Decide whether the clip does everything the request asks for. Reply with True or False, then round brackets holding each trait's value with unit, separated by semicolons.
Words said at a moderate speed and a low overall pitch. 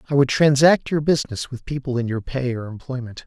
False (220 wpm; 130 Hz)